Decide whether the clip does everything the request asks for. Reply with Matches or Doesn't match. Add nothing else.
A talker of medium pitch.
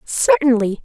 Doesn't match